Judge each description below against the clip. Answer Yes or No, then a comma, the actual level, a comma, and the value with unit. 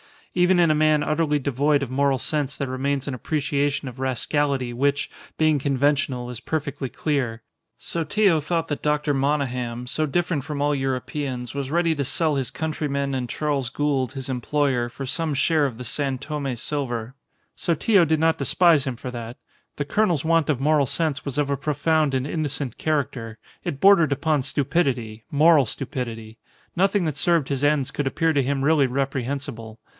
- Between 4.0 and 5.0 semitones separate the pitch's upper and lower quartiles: No, average, 2.9 semitones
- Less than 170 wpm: No, average, 175 wpm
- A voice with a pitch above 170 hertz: No, medium, 140 Hz